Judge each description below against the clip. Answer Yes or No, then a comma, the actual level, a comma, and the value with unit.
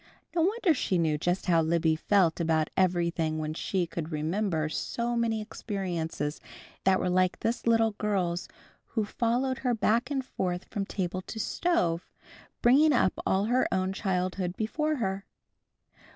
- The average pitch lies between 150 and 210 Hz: Yes, high, 190 Hz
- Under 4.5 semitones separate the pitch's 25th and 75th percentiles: No, average, 5.3 semitones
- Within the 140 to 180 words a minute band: Yes, average, 150 wpm